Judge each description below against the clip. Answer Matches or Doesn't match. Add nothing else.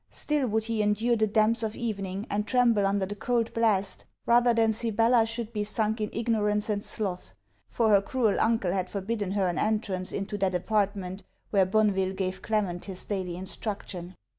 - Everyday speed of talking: Matches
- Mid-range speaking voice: Doesn't match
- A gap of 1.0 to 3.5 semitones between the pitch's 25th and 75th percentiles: Matches